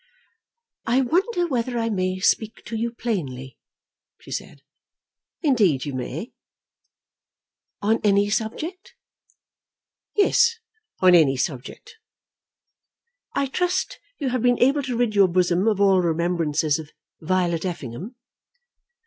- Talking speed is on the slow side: Yes, slow, 115 wpm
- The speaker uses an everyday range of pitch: No, wide, 6.8 semitones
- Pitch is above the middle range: Yes, high, 205 Hz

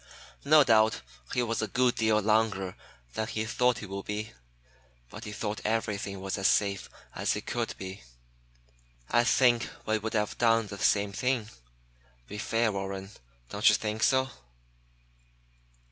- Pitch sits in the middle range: No, low, 110 Hz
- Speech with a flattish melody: Yes, narrow, 2.3 semitones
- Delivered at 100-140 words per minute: No, average, 155 wpm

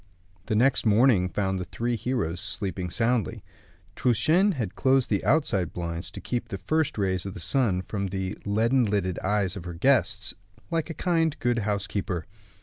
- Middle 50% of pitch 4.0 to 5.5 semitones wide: Yes, average, 5.1 semitones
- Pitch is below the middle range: Yes, low, 105 Hz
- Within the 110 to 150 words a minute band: No, average, 170 wpm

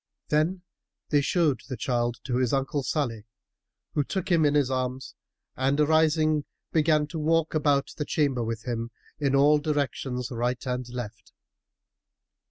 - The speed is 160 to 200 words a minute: No, average, 150 wpm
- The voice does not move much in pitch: No, average, 3.5 semitones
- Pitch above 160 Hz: No, medium, 140 Hz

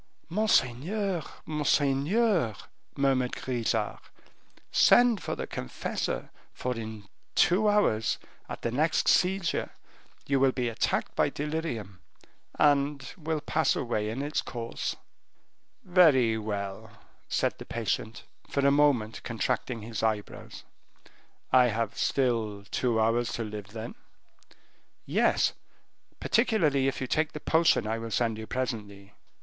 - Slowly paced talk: Yes, slow, 120 wpm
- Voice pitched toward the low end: Yes, low, 125 Hz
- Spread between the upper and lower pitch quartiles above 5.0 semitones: Yes, wide, 5.4 semitones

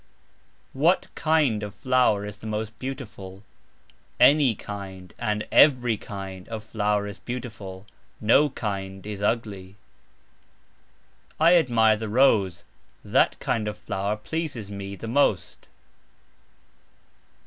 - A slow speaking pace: Yes, slow, 115 wpm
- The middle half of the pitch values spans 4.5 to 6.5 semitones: No, average, 3.9 semitones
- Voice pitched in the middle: No, low, 105 Hz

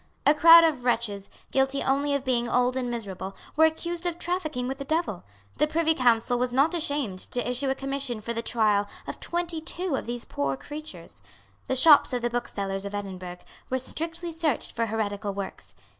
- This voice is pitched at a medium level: No, very high, 255 Hz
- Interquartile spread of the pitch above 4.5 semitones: Yes, wide, 5.6 semitones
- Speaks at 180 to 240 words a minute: Yes, average, 190 wpm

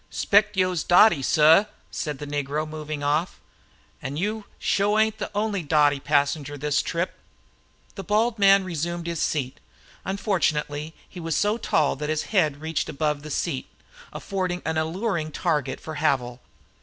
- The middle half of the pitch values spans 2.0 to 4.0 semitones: No, average, 4.6 semitones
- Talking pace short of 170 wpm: Yes, average, 160 wpm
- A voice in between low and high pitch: Yes, medium, 160 Hz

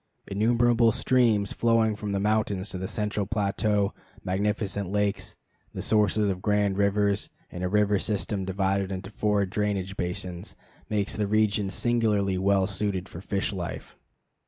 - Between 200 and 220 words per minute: No, average, 145 wpm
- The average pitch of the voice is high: No, low, 100 Hz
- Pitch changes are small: Yes, narrow, 1.6 semitones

